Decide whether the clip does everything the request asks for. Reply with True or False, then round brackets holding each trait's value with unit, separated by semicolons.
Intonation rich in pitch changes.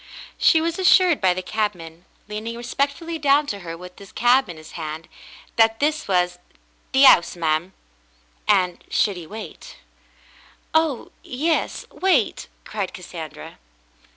True (8.2 semitones)